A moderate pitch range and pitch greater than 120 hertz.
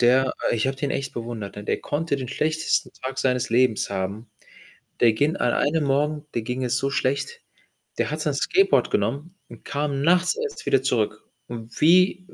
Yes: average, 4.3 semitones; low, 135 Hz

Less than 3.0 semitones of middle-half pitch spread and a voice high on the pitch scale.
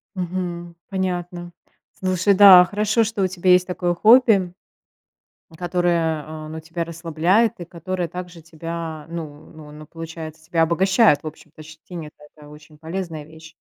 No: narrow, 2.4 semitones; medium, 170 Hz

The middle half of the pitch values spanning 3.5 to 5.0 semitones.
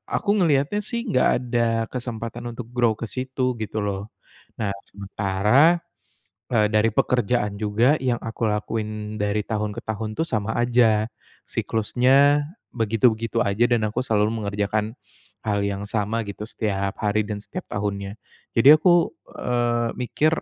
No: average, 2.9 semitones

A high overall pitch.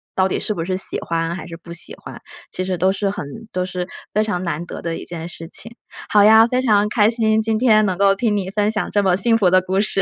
Yes: high, 195 Hz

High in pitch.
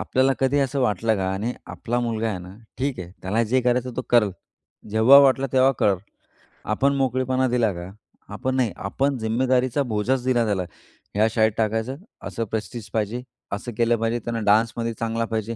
No: low, 115 Hz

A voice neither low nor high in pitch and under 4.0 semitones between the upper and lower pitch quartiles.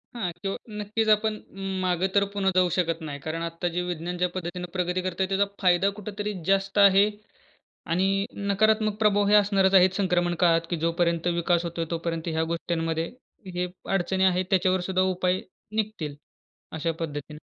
Yes: medium, 180 Hz; average, 2.7 semitones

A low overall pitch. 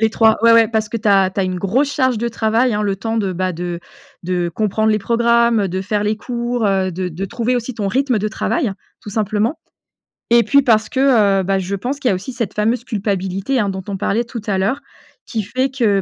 No: high, 215 Hz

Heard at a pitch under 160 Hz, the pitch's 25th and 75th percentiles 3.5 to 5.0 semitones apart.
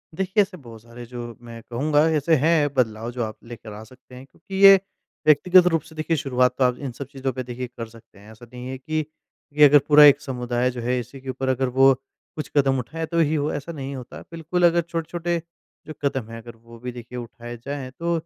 Yes: low, 135 Hz; average, 4.4 semitones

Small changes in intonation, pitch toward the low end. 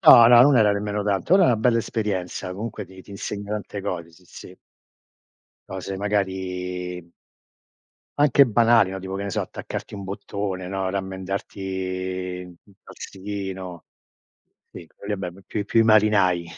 Yes: narrow, 2.1 semitones; very low, 95 Hz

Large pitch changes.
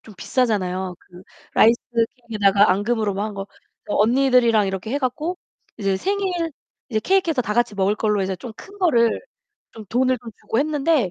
No: average, 4.4 semitones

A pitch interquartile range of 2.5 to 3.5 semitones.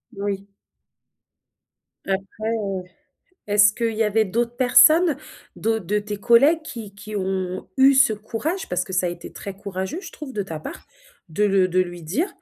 No: average, 3.9 semitones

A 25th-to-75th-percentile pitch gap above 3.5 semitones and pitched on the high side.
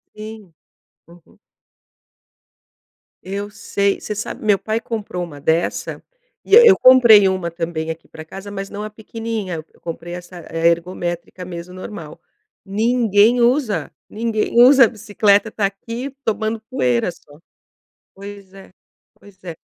Yes: average, 4.1 semitones; high, 200 Hz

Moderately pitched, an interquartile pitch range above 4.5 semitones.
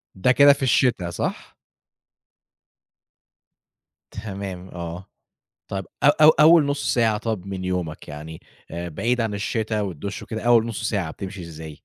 No: low, 100 Hz; average, 4.9 semitones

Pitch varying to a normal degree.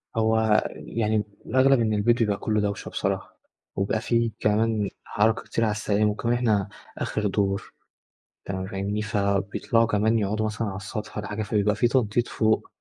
No: narrow, 1.6 semitones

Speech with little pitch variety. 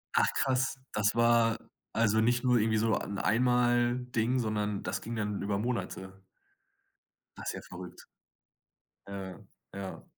No: average, 3.0 semitones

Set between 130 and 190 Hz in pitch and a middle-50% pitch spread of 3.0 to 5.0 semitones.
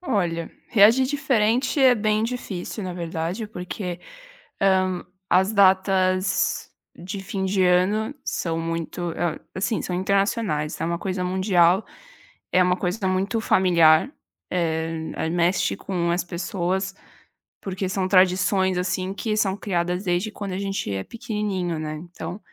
No: medium, 185 Hz; narrow, 2.4 semitones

